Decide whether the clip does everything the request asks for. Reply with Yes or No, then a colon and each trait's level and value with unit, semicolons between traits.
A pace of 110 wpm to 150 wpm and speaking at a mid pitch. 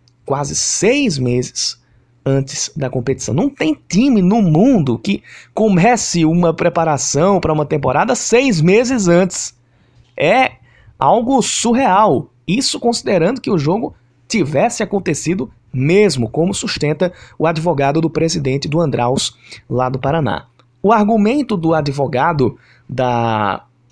Yes: slow, 120 wpm; medium, 155 Hz